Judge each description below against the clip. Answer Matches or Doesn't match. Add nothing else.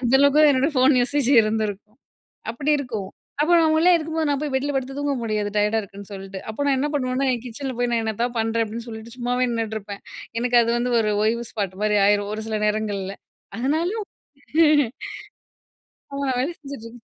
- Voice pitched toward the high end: Matches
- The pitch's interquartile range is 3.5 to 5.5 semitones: Matches